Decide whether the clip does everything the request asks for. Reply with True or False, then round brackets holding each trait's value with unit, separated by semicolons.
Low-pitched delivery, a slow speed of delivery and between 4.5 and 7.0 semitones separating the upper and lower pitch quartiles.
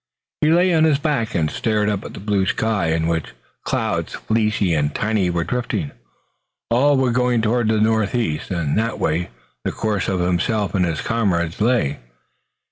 False (105 Hz; 175 wpm; 5.2 semitones)